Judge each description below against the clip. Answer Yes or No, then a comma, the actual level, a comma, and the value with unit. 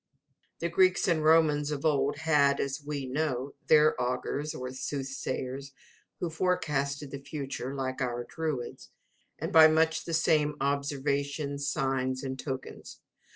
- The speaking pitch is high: No, medium, 140 Hz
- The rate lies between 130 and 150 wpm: Yes, slow, 135 wpm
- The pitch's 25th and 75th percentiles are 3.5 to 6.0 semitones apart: No, narrow, 2.6 semitones